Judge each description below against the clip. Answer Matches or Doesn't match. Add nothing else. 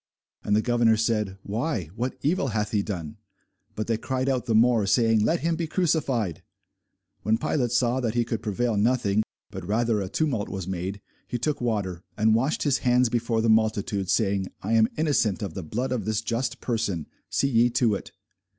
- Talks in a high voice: Doesn't match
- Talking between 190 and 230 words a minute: Matches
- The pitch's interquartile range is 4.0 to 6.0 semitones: Doesn't match